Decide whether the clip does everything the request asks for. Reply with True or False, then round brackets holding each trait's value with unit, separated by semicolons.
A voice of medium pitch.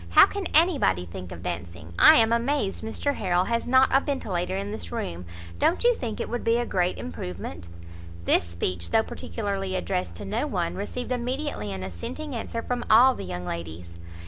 False (195 Hz)